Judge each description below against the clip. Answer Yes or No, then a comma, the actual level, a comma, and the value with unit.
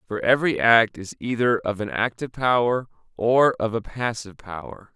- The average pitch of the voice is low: Yes, low, 115 Hz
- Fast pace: No, average, 170 wpm